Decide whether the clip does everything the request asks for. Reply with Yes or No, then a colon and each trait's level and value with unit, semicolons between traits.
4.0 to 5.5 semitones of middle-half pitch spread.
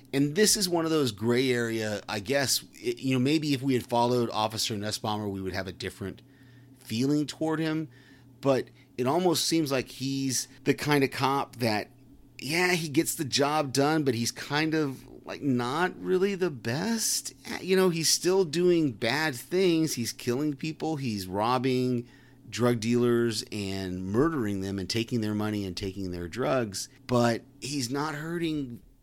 Yes: average, 4.7 semitones